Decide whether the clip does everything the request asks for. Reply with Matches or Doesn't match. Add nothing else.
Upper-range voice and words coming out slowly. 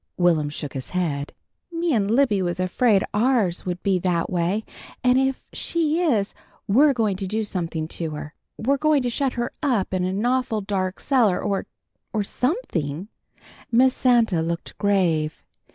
Doesn't match